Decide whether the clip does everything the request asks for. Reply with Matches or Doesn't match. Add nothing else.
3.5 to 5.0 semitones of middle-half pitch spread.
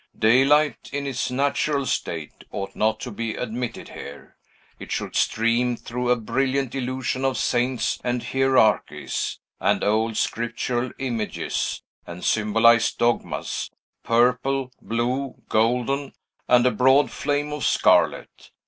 Doesn't match